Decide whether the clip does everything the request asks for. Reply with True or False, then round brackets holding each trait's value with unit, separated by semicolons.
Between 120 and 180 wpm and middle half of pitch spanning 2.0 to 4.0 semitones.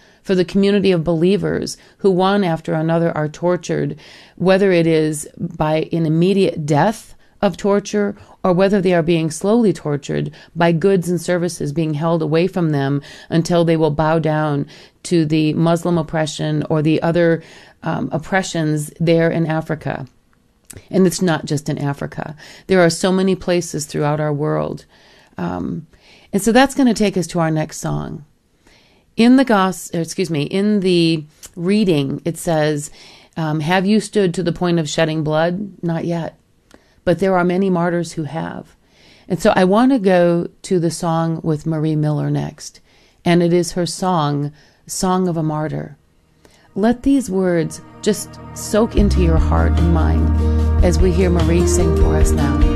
True (170 wpm; 3.5 semitones)